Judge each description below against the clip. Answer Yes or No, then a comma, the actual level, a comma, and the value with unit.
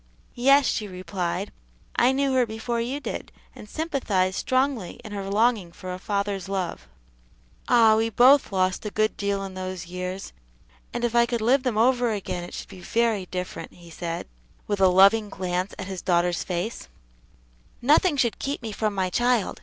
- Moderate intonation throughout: Yes, average, 4.4 semitones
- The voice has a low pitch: No, high, 205 Hz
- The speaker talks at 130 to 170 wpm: No, average, 180 wpm